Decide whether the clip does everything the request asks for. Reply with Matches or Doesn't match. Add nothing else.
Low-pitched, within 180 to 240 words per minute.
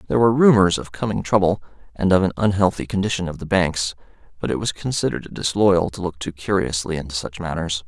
Matches